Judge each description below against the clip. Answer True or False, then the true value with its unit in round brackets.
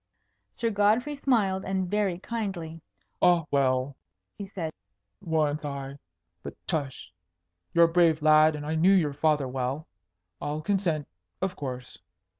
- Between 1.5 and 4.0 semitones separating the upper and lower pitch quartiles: False (4.5 semitones)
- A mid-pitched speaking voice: True (160 Hz)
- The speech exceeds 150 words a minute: False (135 wpm)